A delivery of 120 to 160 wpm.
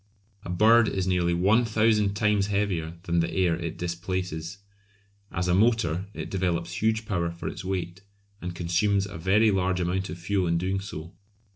No: average, 175 wpm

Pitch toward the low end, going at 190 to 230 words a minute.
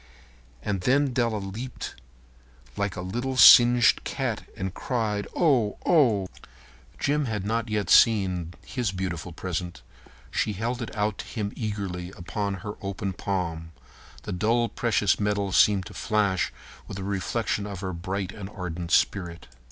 No: low, 100 Hz; average, 150 wpm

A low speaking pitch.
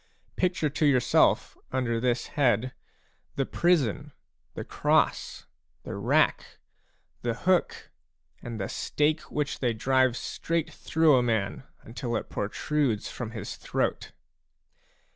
Yes: low, 130 Hz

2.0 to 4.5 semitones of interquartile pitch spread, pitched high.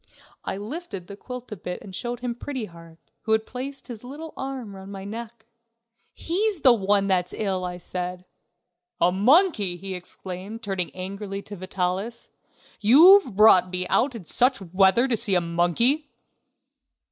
No: average, 5.2 semitones; high, 205 Hz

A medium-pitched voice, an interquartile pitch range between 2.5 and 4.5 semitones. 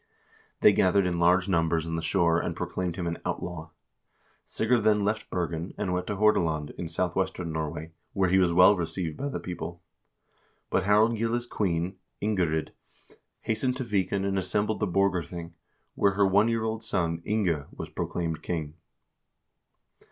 No: very low, 90 Hz; average, 3.6 semitones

